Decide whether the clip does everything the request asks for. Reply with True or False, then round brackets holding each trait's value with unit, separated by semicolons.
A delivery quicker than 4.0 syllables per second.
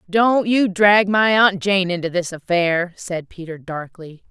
False (3.9 syllables/s)